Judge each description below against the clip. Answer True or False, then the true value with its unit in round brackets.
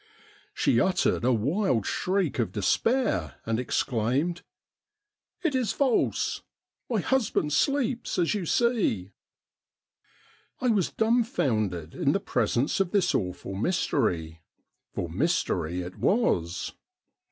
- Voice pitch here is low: False (175 Hz)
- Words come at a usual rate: False (115 wpm)